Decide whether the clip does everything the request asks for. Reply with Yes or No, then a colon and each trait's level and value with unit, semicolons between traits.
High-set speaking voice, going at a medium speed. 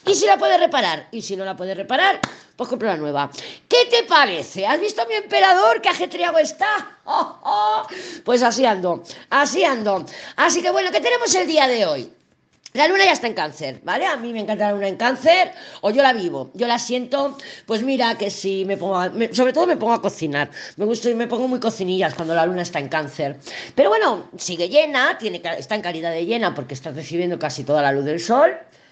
No: high, 230 Hz; fast, 230 wpm